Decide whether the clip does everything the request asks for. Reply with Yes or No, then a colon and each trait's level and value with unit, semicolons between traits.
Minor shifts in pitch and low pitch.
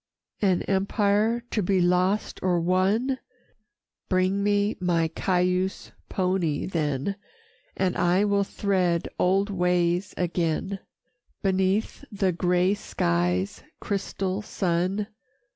No: narrow, 2.1 semitones; medium, 185 Hz